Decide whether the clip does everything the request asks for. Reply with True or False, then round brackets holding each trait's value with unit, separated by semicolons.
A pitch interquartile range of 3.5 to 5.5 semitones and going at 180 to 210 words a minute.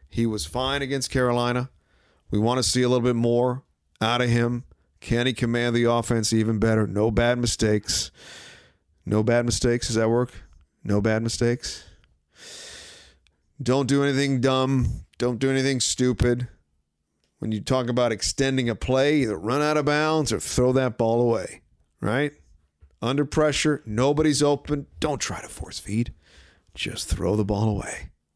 False (3.9 semitones; 160 wpm)